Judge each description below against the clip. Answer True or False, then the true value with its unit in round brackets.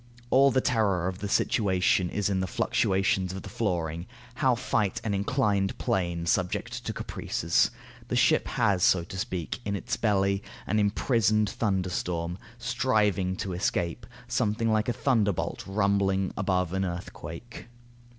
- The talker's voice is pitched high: False (95 Hz)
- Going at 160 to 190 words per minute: False (145 wpm)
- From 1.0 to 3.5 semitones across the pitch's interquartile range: True (2.8 semitones)